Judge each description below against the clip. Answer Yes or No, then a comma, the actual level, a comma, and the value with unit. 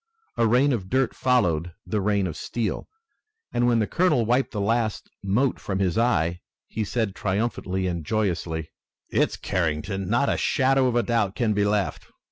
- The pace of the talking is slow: No, average, 170 wpm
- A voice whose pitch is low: Yes, low, 105 Hz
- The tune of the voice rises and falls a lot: No, average, 4.2 semitones